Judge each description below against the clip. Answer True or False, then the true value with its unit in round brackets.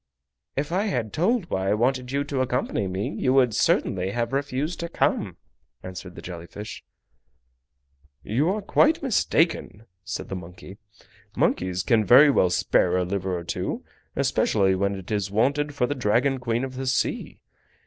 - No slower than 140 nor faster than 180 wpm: True (170 wpm)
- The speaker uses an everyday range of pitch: False (6.6 semitones)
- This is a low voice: True (120 Hz)